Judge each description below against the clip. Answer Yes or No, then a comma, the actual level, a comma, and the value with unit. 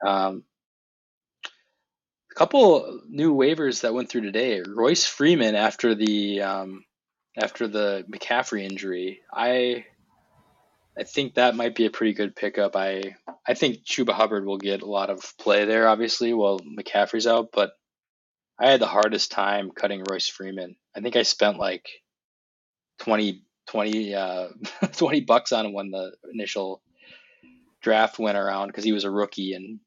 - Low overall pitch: Yes, low, 100 Hz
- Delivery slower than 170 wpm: Yes, average, 155 wpm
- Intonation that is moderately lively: No, narrow, 2.3 semitones